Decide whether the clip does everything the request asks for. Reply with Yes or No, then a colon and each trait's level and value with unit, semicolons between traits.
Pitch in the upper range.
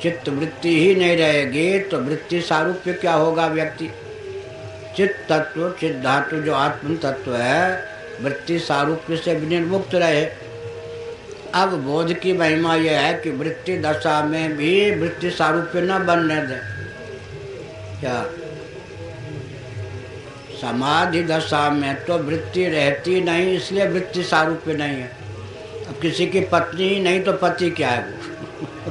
No: medium, 160 Hz